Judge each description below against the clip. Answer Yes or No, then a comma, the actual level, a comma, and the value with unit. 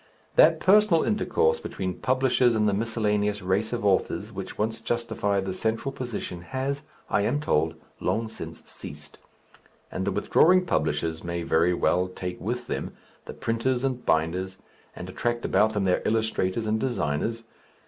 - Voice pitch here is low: Yes, low, 110 Hz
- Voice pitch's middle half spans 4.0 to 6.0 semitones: Yes, average, 4.8 semitones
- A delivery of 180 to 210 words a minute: No, average, 155 wpm